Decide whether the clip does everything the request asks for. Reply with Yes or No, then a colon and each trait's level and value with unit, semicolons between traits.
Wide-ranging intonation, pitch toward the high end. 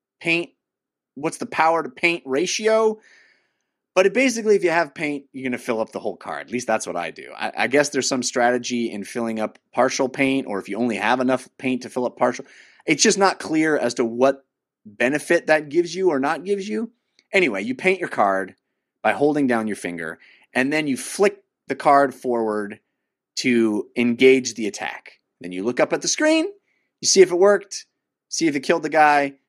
No: wide, 7.5 semitones; medium, 140 Hz